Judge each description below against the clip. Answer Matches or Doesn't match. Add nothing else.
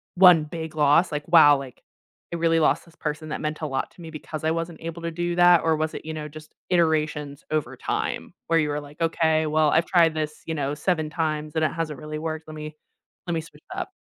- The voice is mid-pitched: Matches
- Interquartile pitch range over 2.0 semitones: Doesn't match